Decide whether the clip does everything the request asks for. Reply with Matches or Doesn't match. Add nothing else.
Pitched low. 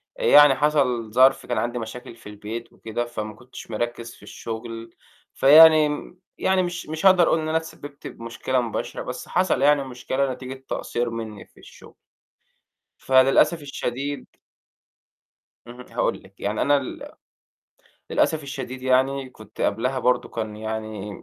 Matches